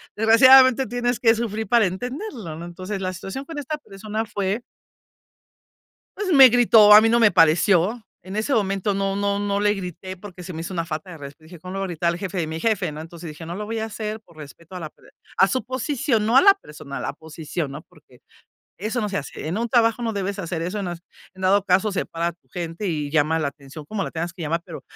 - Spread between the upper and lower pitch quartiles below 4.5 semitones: No, average, 4.8 semitones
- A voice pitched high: Yes, high, 195 Hz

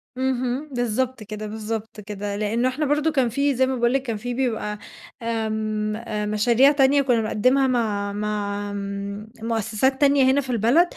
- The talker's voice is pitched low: No, high, 230 Hz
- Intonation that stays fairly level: No, average, 3.7 semitones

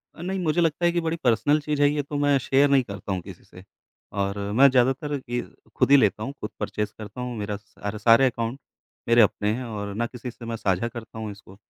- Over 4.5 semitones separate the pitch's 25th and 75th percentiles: Yes, average, 5.0 semitones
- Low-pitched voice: Yes, low, 120 Hz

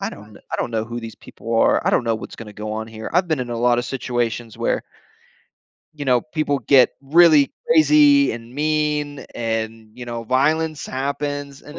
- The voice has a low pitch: Yes, low, 130 Hz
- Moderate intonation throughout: Yes, average, 4.4 semitones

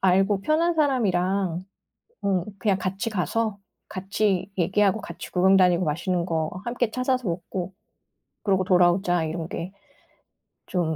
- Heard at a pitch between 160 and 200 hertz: Yes, high, 190 Hz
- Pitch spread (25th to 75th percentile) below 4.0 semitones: Yes, average, 2.8 semitones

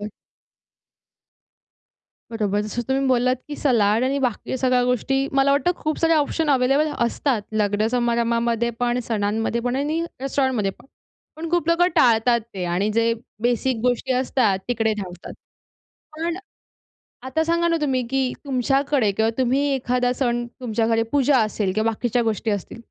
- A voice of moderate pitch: No, high, 245 Hz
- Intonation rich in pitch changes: No, average, 3.3 semitones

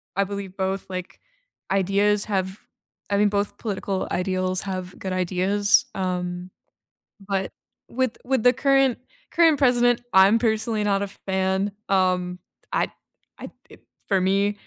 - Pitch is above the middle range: Yes, high, 195 Hz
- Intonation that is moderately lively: No, narrow, 2.0 semitones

